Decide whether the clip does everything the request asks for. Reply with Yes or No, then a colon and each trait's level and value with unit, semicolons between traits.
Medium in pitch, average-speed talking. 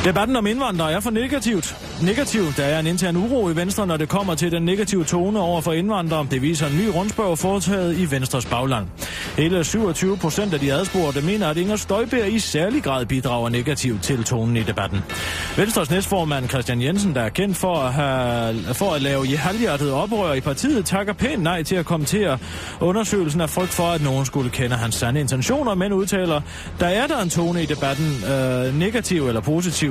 Yes: medium, 170 Hz; average, 200 wpm